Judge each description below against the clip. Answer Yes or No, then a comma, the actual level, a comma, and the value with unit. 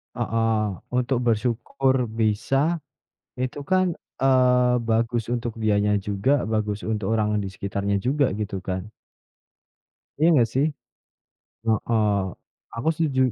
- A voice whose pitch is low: Yes, low, 115 Hz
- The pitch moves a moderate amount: Yes, average, 3.7 semitones